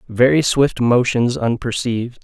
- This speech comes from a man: Yes, male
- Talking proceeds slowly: Yes, slow, 105 wpm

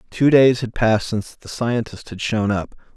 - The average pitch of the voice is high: No, low, 115 Hz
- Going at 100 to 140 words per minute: No, fast, 205 wpm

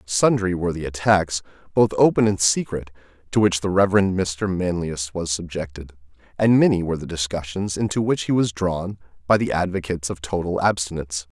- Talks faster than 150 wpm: Yes, average, 170 wpm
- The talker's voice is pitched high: No, very low, 90 Hz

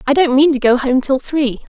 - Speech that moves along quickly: Yes, fast, 275 wpm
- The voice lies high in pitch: Yes, very high, 270 Hz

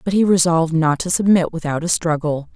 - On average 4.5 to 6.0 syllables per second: Yes, 5.8 syllables/s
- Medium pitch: Yes, medium, 170 Hz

